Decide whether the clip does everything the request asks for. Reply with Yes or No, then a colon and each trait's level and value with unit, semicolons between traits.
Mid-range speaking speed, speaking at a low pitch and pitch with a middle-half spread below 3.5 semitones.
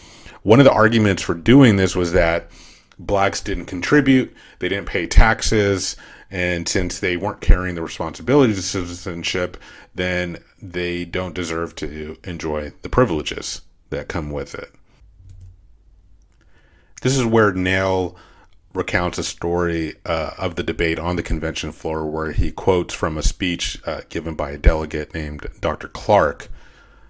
Yes: average, 145 wpm; very low, 90 Hz; narrow, 2.4 semitones